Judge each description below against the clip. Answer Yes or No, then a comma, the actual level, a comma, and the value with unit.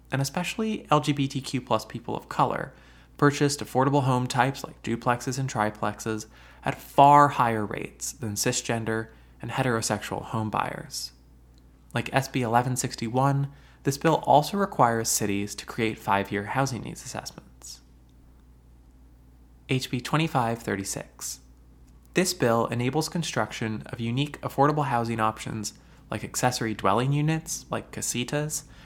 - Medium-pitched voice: No, low, 120 Hz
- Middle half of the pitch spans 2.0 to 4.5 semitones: No, average, 5.2 semitones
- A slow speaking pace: Yes, slow, 120 wpm